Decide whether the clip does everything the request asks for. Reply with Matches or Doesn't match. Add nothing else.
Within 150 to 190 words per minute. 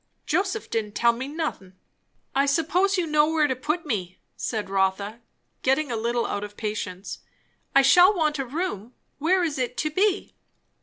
Matches